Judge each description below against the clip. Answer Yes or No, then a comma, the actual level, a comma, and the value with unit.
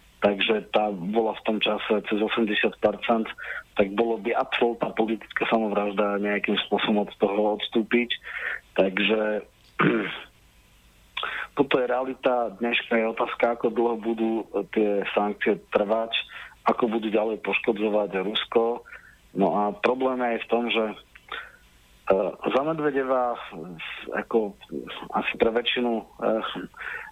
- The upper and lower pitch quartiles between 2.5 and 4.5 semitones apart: No, narrow, 2.1 semitones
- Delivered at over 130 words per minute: No, slow, 110 wpm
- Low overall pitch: Yes, low, 115 Hz